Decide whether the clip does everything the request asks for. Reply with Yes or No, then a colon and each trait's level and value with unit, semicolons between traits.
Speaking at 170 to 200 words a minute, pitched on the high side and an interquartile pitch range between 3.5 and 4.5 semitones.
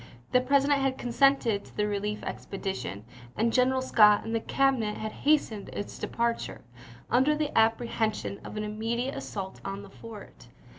No: average, 155 wpm; high, 225 Hz; average, 3.8 semitones